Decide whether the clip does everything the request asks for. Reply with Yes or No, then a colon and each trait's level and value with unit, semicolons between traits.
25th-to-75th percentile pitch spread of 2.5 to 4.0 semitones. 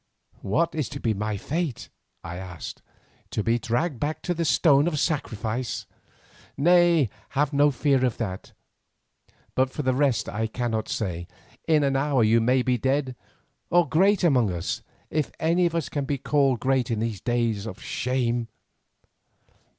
No: average, 4.8 semitones